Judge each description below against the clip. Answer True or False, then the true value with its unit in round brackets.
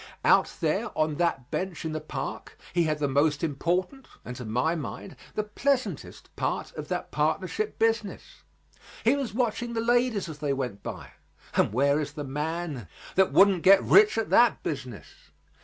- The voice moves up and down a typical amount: False (7.2 semitones)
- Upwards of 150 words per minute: True (175 wpm)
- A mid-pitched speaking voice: True (165 Hz)